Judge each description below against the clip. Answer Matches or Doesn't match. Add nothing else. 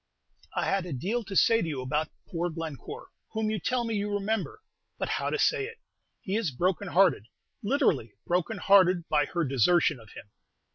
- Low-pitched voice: Doesn't match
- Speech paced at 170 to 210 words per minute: Matches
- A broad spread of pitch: Matches